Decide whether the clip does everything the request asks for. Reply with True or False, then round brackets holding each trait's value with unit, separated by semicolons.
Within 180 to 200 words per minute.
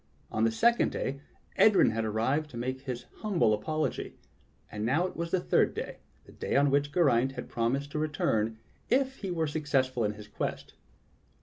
True (195 wpm)